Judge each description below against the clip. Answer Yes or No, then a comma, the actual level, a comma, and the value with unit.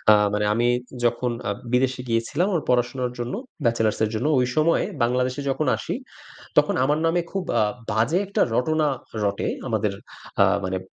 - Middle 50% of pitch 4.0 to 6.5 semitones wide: Yes, average, 4.5 semitones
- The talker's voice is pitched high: No, low, 125 Hz